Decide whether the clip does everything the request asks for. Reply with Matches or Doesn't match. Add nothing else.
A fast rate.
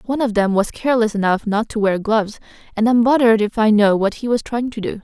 Matches